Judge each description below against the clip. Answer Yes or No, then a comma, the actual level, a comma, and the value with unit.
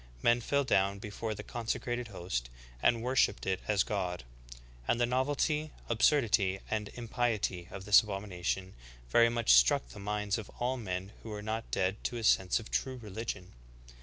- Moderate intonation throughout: Yes, average, 3.6 semitones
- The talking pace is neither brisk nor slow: Yes, average, 165 wpm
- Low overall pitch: Yes, low, 105 Hz